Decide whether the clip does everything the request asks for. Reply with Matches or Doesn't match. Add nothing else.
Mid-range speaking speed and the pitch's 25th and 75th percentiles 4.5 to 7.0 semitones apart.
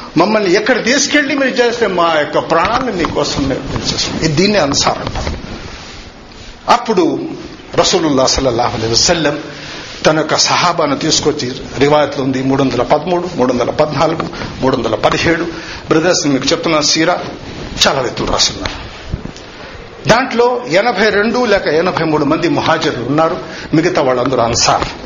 Matches